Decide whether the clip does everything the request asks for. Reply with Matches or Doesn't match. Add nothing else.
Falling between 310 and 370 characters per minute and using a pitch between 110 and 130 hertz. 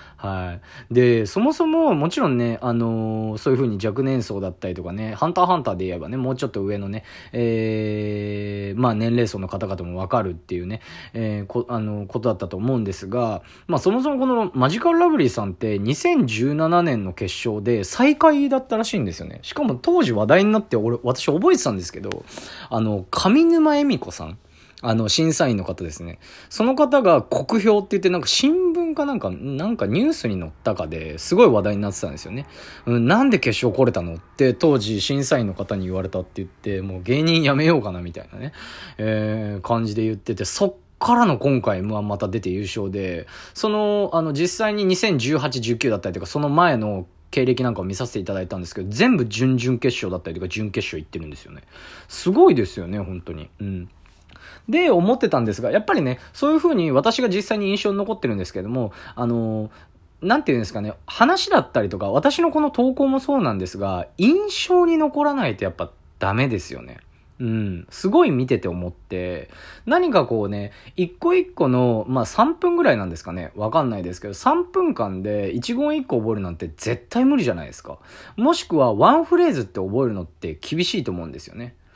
Doesn't match